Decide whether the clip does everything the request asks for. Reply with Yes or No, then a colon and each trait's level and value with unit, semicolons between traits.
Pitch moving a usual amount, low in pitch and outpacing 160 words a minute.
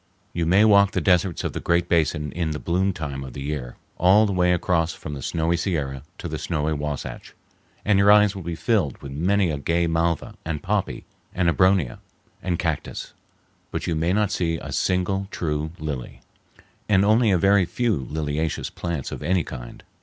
Yes: average, 4.0 semitones; very low, 85 Hz; average, 190 wpm